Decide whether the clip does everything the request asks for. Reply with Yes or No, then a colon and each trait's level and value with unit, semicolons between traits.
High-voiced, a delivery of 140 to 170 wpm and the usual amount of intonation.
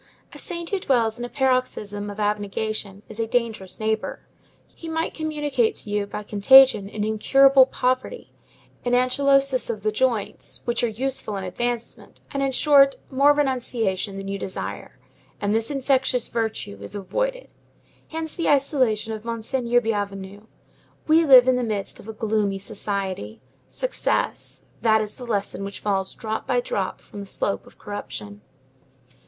Yes: high, 225 Hz; average, 160 wpm; average, 4.5 semitones